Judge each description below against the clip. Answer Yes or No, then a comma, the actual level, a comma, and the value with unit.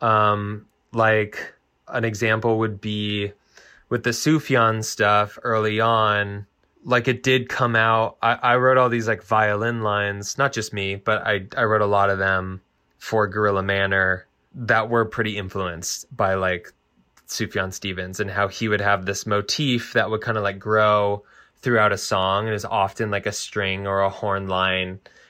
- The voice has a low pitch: Yes, low, 105 Hz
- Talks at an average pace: Yes, average, 175 wpm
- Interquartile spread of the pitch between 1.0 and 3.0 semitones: Yes, narrow, 2.4 semitones